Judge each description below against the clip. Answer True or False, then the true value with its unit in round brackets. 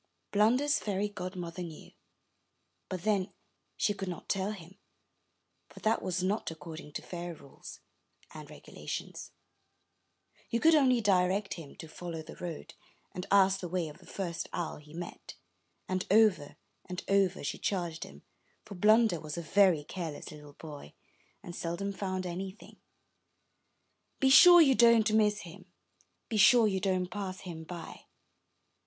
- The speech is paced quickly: False (150 wpm)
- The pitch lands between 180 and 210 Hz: True (185 Hz)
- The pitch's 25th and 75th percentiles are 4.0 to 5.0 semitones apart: False (3.5 semitones)